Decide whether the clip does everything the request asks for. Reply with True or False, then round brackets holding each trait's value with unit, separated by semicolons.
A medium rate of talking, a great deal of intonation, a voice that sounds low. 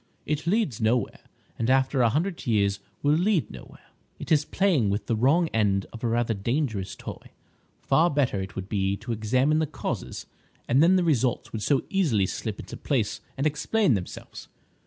True (180 wpm; 6.4 semitones; 125 Hz)